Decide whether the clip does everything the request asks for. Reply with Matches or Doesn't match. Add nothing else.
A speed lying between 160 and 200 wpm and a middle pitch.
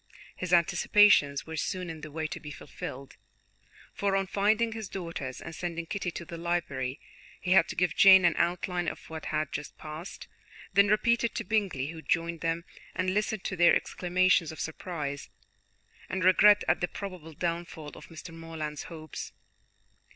Matches